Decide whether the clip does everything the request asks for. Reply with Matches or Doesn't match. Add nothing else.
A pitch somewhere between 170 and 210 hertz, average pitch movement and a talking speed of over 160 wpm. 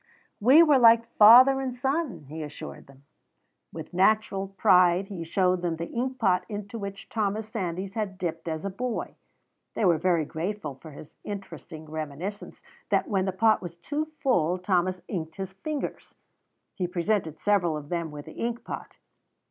Matches